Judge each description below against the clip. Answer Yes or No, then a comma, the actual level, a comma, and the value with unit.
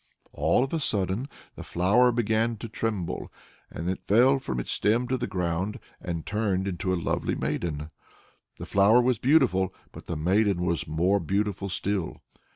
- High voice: No, low, 100 Hz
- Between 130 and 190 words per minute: Yes, average, 165 wpm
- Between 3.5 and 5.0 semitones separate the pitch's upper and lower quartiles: Yes, average, 4.4 semitones